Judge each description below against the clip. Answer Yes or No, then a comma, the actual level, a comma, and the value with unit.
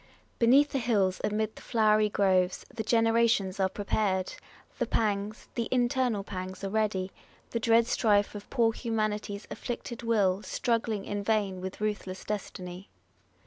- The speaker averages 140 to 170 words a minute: Yes, average, 145 wpm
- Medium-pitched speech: No, high, 210 Hz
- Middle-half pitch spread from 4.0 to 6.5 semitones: No, average, 2.8 semitones